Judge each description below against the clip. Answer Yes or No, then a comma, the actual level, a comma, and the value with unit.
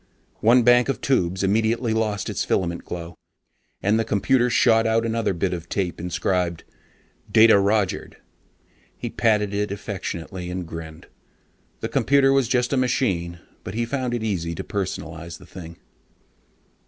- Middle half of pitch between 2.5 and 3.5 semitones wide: No, average, 4.8 semitones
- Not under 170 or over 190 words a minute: No, average, 150 wpm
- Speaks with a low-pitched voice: Yes, low, 100 Hz